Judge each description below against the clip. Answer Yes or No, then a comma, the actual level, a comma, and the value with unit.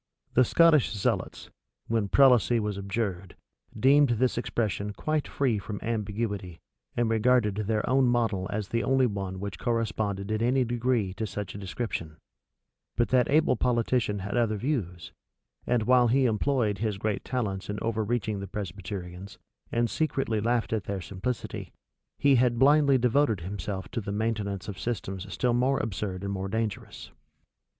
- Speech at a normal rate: Yes, average, 155 wpm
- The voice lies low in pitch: Yes, low, 110 Hz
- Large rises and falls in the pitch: No, average, 3.6 semitones